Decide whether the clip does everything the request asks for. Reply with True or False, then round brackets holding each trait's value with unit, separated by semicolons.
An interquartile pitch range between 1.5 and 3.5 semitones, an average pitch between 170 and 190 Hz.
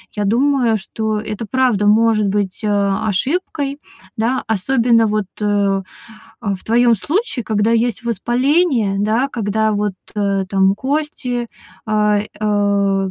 False (3.1 semitones; 220 Hz)